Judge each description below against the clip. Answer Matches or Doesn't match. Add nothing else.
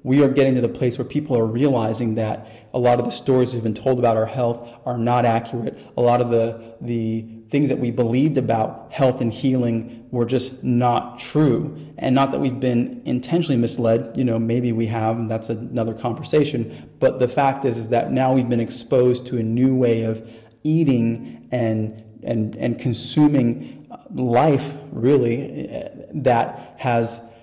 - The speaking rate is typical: Matches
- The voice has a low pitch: Matches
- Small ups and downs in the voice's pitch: Matches